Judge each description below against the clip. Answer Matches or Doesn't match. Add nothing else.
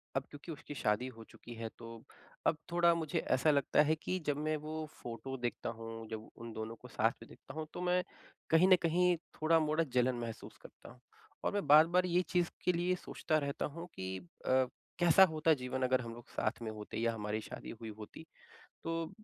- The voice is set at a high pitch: Doesn't match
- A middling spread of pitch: Doesn't match